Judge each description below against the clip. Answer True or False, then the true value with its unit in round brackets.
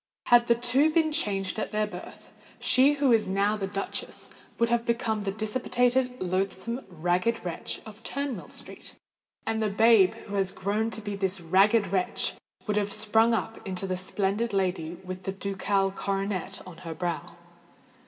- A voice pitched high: True (205 Hz)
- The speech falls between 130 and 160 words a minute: False (170 wpm)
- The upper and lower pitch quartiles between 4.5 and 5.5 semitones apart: False (3.4 semitones)